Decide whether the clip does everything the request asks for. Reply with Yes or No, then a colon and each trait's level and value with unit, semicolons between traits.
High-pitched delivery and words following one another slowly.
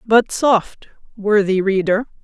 Yes: high, 205 Hz; slow, 105 wpm